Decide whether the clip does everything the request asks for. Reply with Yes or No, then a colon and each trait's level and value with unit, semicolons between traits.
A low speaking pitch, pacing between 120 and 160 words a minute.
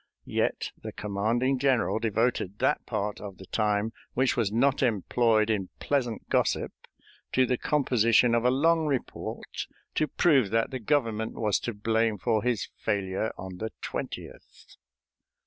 Yes: low, 115 Hz; average, 145 wpm